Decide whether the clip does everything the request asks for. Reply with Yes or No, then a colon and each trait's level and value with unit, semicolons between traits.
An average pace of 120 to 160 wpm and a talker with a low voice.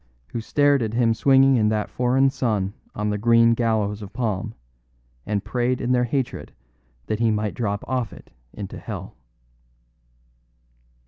Yes: average, 150 wpm; low, 115 Hz